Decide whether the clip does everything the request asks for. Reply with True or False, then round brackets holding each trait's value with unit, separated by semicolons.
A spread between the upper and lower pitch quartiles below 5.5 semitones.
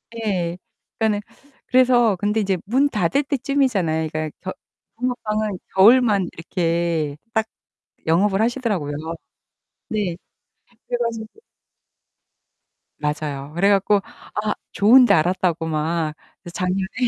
True (5.1 semitones)